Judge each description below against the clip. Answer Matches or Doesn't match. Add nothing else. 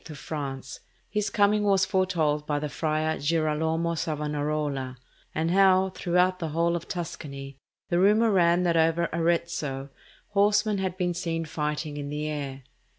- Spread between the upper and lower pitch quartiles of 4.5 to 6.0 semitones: Doesn't match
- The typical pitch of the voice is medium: Matches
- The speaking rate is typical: Matches